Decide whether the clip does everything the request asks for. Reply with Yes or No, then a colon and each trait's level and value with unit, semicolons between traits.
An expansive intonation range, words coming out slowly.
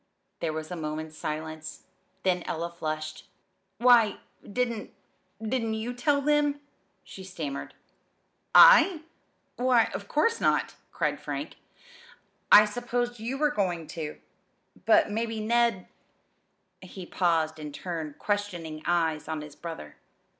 Yes: wide, 7.2 semitones; slow, 125 wpm